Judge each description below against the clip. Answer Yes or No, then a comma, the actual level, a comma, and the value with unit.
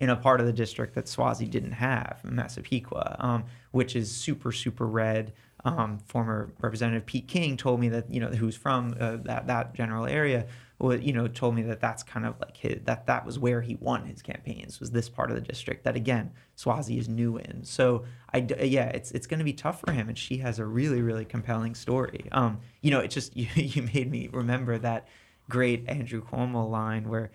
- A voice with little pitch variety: Yes, narrow, 2.0 semitones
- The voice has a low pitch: Yes, low, 120 Hz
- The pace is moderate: No, fast, 215 wpm